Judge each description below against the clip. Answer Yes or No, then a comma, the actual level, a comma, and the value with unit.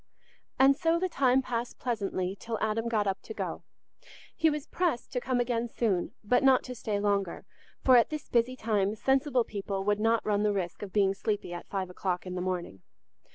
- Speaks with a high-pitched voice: Yes, high, 220 Hz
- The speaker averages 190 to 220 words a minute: Yes, average, 200 wpm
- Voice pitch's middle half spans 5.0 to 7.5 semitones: No, average, 4.3 semitones